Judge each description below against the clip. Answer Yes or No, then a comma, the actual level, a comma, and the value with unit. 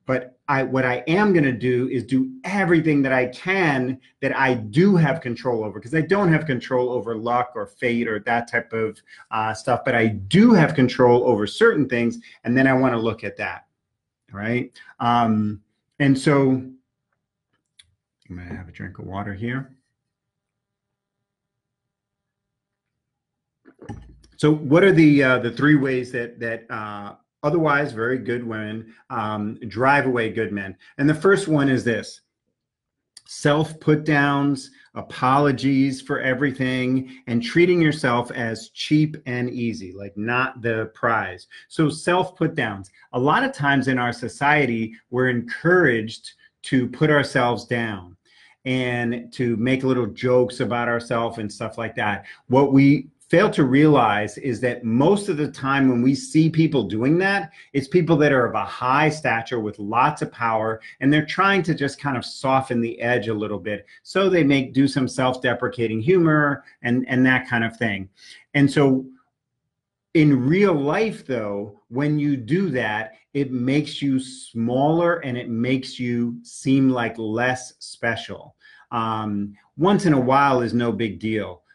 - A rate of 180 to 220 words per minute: No, average, 165 wpm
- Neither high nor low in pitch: No, low, 130 Hz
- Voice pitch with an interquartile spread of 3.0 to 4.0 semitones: Yes, average, 3.6 semitones